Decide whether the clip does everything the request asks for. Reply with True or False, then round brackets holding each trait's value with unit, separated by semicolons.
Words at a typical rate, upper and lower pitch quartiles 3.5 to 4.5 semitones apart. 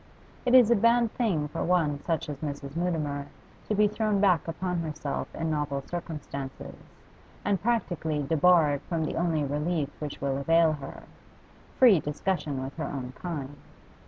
True (160 wpm; 3.8 semitones)